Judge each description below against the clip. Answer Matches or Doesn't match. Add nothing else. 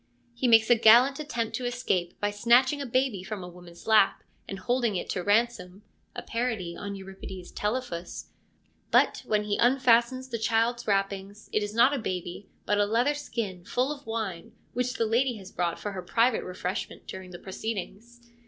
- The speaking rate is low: Doesn't match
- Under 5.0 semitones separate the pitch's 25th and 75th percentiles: Matches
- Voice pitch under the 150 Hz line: Doesn't match